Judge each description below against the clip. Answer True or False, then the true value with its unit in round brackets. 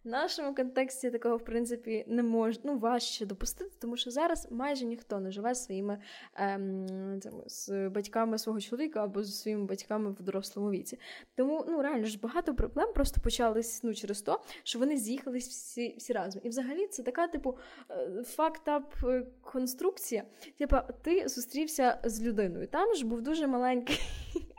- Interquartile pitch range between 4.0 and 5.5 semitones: True (4.3 semitones)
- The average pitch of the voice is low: False (245 Hz)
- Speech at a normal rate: False (160 wpm)